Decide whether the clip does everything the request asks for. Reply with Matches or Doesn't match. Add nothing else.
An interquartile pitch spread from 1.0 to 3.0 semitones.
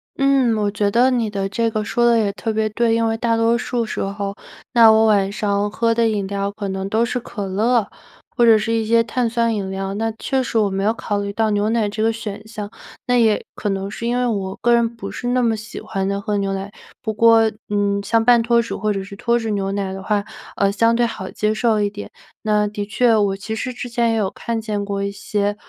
Matches